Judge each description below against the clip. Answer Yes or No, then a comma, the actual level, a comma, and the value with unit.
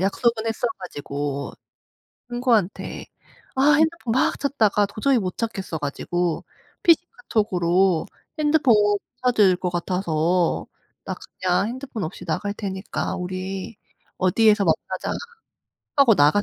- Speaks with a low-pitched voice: No, high, 200 Hz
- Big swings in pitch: No, average, 4.9 semitones